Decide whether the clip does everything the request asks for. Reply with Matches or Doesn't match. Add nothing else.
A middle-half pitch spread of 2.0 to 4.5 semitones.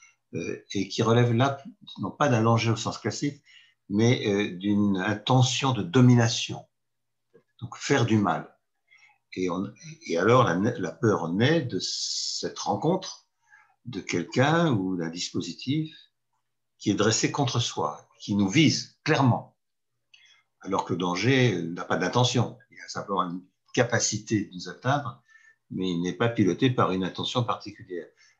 Doesn't match